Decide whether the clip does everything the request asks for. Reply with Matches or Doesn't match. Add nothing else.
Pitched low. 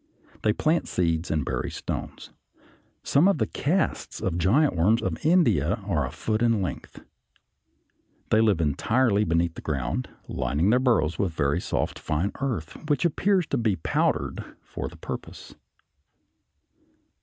Matches